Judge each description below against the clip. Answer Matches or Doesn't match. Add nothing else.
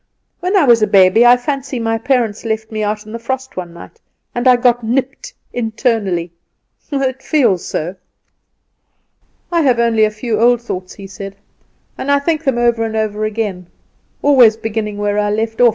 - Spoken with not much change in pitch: Doesn't match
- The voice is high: Matches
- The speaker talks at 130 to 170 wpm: Doesn't match